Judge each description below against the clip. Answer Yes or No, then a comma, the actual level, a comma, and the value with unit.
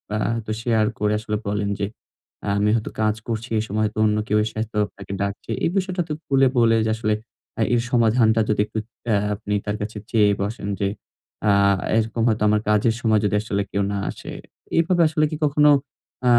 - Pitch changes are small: Yes, narrow, 1.8 semitones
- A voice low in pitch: Yes, low, 110 Hz